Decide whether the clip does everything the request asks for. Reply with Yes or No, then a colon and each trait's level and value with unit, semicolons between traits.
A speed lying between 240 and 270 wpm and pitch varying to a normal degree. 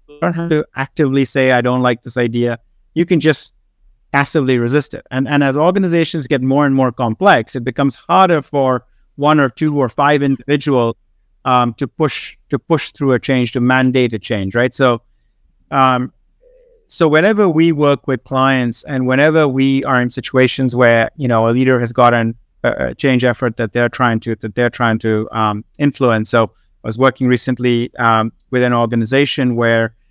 No: average, 185 wpm; average, 3.1 semitones